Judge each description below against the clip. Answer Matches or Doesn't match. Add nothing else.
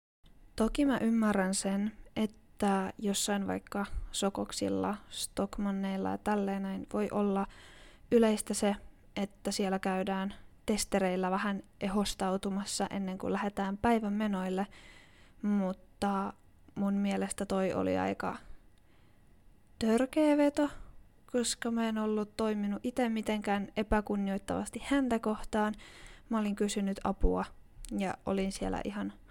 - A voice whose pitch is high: Matches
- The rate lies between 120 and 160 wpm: Doesn't match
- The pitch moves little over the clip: Matches